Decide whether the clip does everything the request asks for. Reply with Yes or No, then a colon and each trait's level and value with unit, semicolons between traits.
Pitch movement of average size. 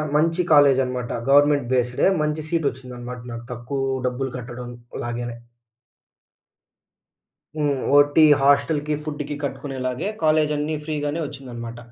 Yes: average, 3.2 semitones